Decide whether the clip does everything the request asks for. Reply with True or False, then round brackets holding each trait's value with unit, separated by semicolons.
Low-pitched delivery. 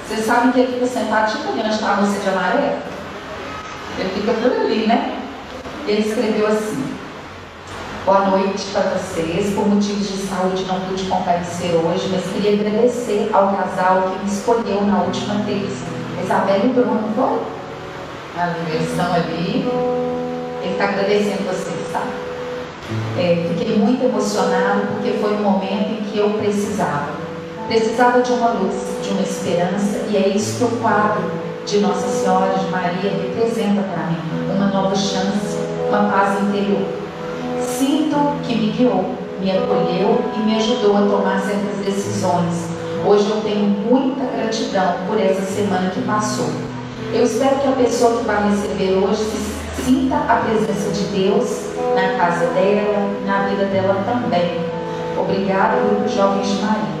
False (205 Hz)